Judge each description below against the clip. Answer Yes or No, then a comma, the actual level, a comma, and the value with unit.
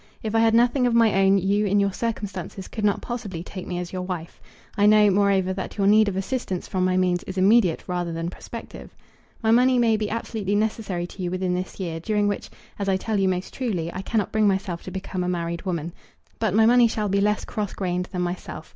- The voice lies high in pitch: Yes, high, 195 Hz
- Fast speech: Yes, fast, 235 wpm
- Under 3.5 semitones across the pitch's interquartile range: Yes, average, 2.9 semitones